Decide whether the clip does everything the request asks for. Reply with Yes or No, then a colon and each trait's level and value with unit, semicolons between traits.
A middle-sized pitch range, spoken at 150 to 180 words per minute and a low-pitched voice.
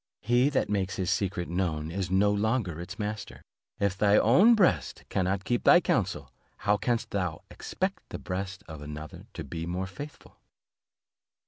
Yes: average, 3.2 semitones; average, 160 wpm; very low, 95 Hz